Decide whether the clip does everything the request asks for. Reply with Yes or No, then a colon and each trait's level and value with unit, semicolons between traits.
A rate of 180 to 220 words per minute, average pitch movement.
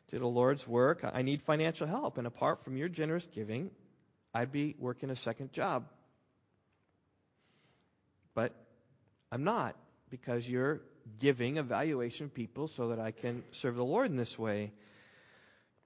No: average, 150 wpm; average, 3.4 semitones